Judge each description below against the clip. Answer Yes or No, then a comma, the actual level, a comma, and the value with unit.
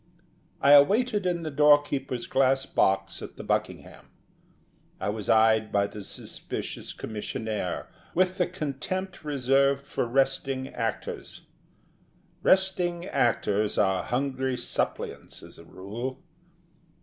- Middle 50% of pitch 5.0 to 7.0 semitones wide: Yes, average, 5.3 semitones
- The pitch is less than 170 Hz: Yes, low, 135 Hz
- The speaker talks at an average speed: No, slow, 115 wpm